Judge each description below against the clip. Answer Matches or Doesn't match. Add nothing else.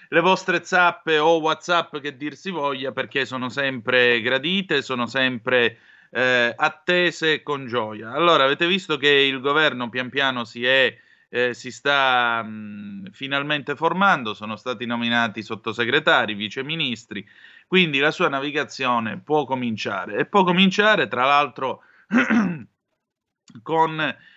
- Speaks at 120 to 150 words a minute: Matches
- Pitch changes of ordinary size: Matches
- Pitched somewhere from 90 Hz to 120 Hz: Doesn't match